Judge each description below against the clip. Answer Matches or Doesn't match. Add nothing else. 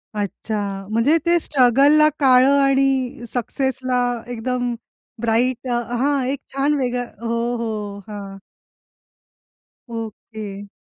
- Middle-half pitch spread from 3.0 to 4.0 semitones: Matches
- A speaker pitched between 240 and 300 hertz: Matches